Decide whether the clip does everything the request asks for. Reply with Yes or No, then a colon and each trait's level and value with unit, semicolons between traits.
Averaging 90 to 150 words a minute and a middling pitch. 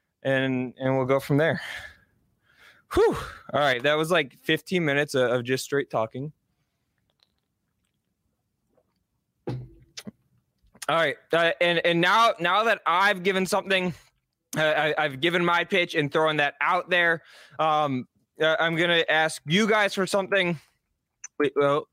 Yes: average, 140 wpm; medium, 160 Hz